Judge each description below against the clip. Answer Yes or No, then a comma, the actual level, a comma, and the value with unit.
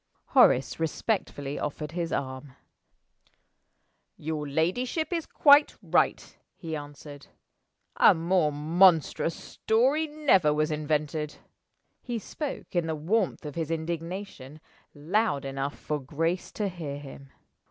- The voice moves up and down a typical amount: Yes, average, 4.5 semitones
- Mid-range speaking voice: Yes, medium, 160 Hz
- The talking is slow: Yes, slow, 115 wpm